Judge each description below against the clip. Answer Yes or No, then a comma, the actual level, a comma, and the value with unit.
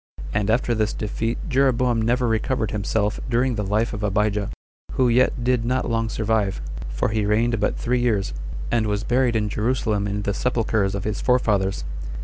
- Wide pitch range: No, narrow, 2.6 semitones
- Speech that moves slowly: No, average, 175 wpm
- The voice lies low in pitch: Yes, low, 110 Hz